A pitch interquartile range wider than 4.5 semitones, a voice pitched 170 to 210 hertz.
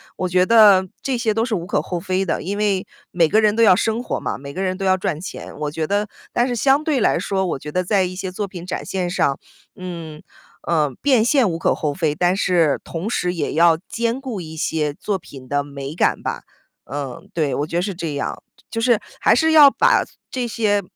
Yes: average, 5.1 semitones; medium, 185 Hz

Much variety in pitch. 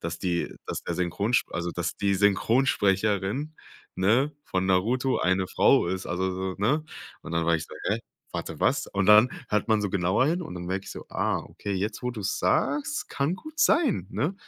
Yes: wide, 5.7 semitones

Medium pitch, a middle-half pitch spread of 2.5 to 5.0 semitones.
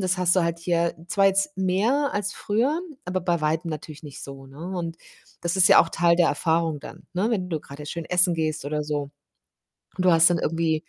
Yes: medium, 170 Hz; average, 2.8 semitones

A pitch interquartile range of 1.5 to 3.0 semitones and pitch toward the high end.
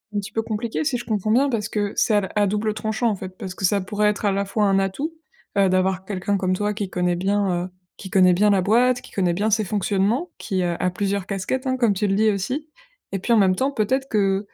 Yes: narrow, 2.4 semitones; high, 205 Hz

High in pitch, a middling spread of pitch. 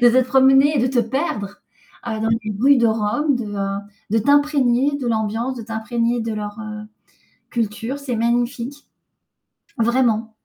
Yes: high, 235 Hz; average, 3.2 semitones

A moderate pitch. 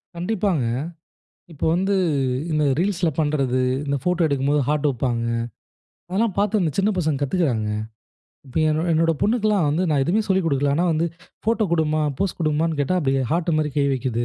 Yes: medium, 155 Hz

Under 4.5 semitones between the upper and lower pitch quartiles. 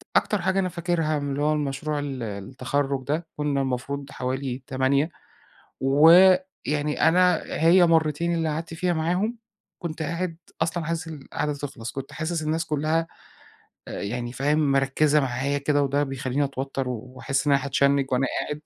Yes: average, 3.2 semitones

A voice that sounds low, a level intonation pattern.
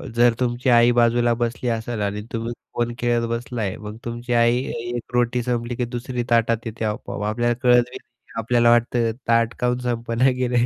Yes: low, 120 Hz; narrow, 0.8 semitones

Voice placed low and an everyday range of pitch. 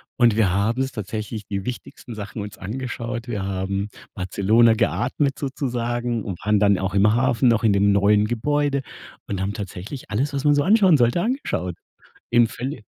Yes: low, 115 Hz; average, 4.1 semitones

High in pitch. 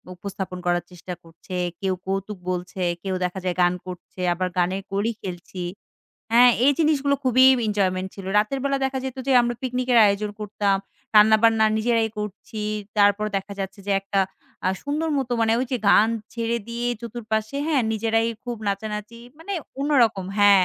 Yes: high, 210 Hz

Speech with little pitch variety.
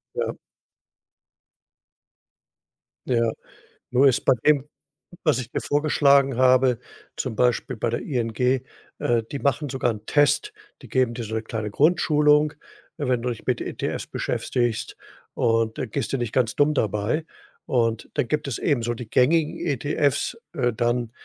No: average, 3.7 semitones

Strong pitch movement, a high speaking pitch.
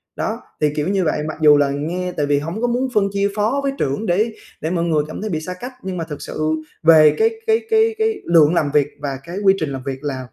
No: wide, 5.9 semitones; medium, 165 Hz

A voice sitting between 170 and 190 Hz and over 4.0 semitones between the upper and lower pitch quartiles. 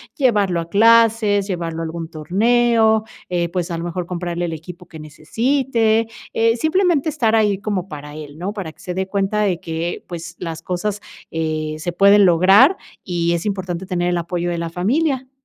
Yes: medium, 185 Hz; average, 4.5 semitones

